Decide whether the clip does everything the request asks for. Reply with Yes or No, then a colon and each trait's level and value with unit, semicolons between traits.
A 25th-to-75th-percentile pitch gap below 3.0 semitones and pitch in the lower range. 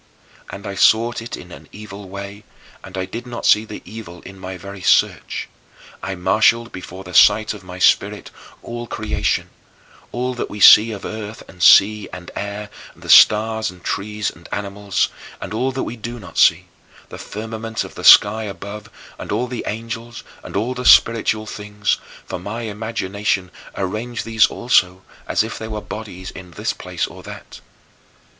Yes: narrow, 2.6 semitones; low, 105 Hz